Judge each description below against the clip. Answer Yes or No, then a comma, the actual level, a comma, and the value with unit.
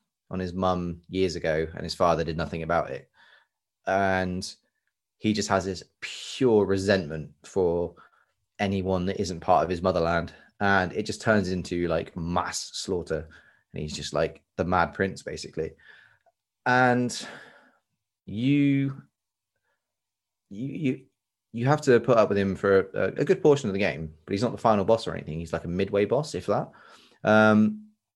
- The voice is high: No, very low, 95 Hz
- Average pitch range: Yes, average, 3.3 semitones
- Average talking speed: Yes, average, 165 wpm